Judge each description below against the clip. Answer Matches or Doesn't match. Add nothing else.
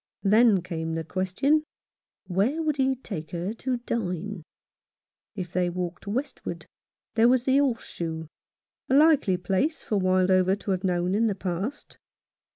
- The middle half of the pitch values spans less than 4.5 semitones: Doesn't match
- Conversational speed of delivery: Matches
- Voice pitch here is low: Doesn't match